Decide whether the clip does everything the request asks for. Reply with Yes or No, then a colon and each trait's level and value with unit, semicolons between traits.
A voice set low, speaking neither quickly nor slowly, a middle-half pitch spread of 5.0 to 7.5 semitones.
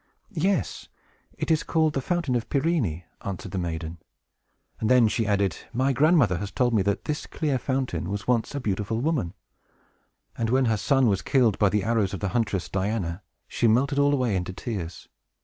Yes: low, 115 Hz; average, 185 wpm; wide, 5.6 semitones